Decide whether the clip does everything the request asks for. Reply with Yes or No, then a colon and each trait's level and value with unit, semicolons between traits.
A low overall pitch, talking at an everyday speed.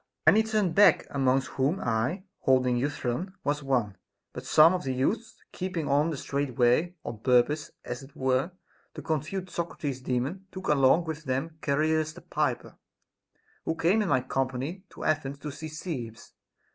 No: medium, 145 Hz; average, 170 wpm